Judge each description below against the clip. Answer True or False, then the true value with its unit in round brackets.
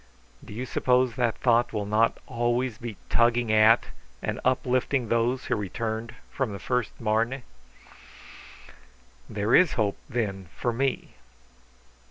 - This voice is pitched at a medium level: False (115 Hz)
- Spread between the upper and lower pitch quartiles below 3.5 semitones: True (2.4 semitones)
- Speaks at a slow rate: True (130 wpm)